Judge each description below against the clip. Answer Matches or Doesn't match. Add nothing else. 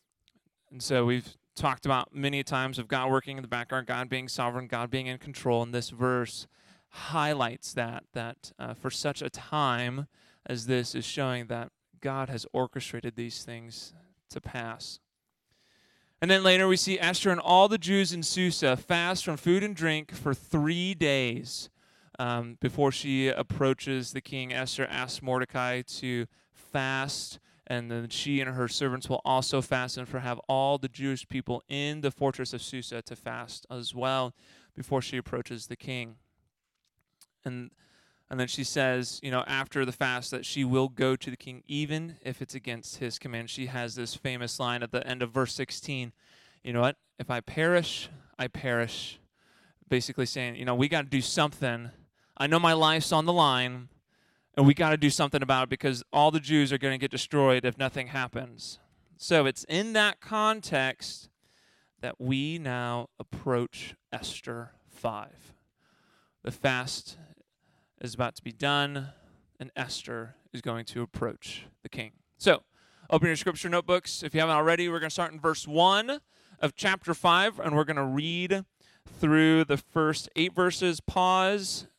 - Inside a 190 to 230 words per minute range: Doesn't match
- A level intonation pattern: Doesn't match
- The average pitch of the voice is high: Doesn't match